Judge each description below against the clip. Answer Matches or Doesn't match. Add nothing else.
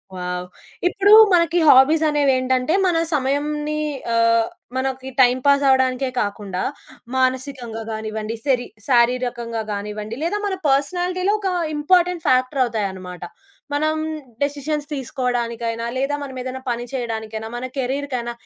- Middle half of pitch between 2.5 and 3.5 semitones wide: Doesn't match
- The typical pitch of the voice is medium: Doesn't match